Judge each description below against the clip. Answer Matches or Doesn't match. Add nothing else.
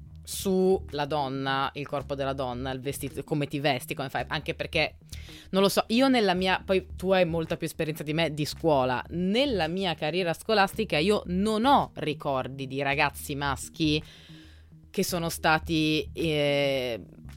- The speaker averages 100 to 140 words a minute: Doesn't match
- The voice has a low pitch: Doesn't match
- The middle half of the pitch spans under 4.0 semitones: Doesn't match